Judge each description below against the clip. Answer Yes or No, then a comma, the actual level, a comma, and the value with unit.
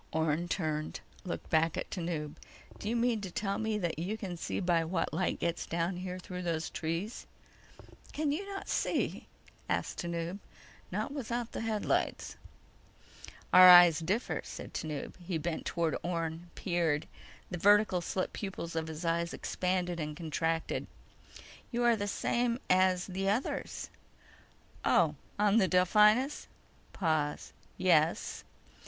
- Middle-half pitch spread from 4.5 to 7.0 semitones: No, average, 3.8 semitones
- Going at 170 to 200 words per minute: No, average, 140 wpm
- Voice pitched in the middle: Yes, medium, 180 Hz